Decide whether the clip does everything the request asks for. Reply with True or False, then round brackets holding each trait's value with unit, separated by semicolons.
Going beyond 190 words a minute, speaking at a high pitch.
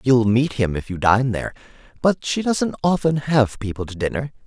False (200 wpm; 125 Hz)